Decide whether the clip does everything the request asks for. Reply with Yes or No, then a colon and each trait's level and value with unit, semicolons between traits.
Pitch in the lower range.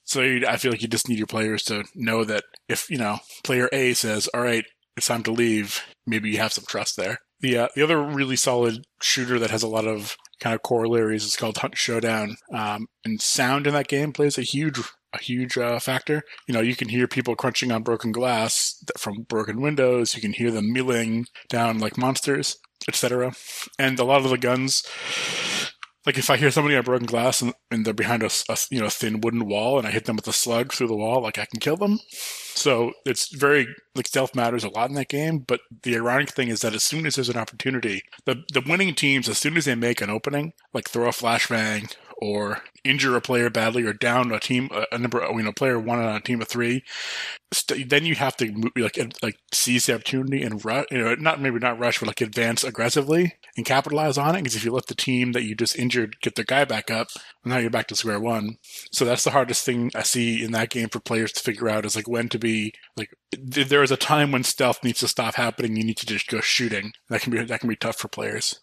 Yes: low, 120 Hz